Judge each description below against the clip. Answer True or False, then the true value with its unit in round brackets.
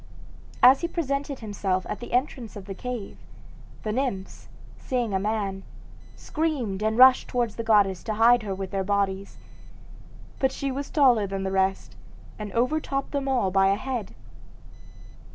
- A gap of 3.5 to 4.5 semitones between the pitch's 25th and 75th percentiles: False (5.0 semitones)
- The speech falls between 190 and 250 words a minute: False (160 wpm)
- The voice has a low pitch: False (220 Hz)